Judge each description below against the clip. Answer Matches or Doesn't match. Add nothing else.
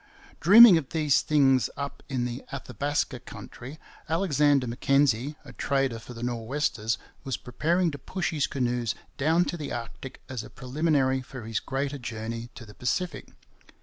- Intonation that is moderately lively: Matches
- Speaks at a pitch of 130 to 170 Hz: Matches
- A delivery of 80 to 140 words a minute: Doesn't match